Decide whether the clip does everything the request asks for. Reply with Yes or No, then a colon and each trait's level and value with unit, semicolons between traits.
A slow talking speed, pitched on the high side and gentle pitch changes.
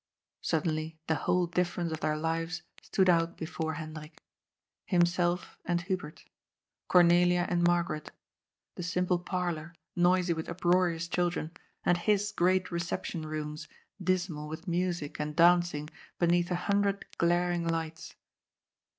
No: slow, 130 wpm; medium, 175 Hz; narrow, 1.7 semitones